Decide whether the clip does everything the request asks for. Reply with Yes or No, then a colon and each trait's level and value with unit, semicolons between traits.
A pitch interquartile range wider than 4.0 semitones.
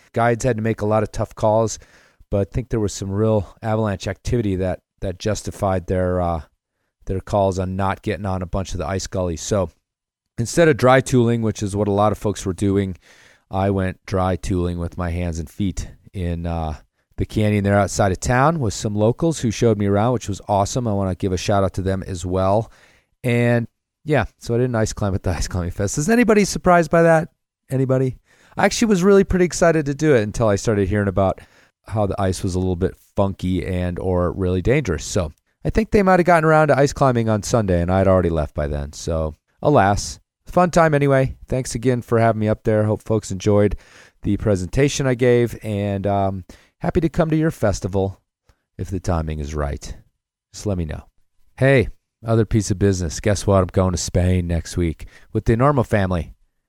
Yes: average, 4.4 semitones